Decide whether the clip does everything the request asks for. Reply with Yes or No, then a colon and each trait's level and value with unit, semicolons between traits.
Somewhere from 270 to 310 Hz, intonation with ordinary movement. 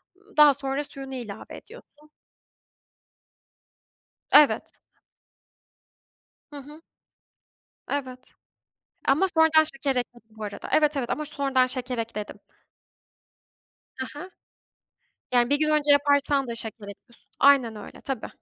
Yes: very high, 275 Hz; average, 3.3 semitones